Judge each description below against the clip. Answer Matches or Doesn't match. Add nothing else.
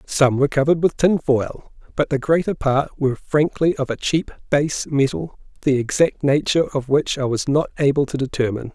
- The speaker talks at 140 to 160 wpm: Doesn't match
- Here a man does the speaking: Matches